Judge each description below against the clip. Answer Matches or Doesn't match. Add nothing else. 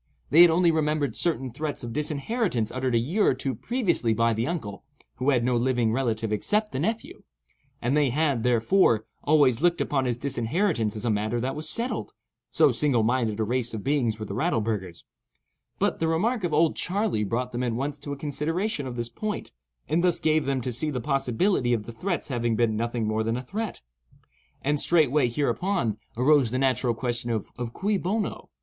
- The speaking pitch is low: Matches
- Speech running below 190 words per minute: Doesn't match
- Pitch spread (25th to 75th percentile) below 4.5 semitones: Doesn't match